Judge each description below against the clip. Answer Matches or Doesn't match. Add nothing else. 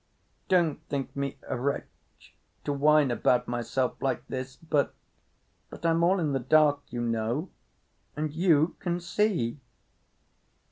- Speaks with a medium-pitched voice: Matches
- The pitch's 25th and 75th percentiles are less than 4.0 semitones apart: Doesn't match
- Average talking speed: Doesn't match